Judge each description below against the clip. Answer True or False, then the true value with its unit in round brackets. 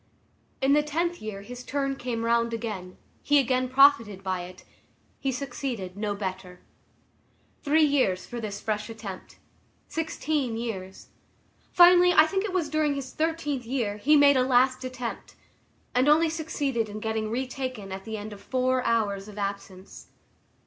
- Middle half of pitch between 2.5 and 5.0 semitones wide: False (5.4 semitones)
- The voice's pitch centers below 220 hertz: False (245 Hz)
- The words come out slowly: False (155 wpm)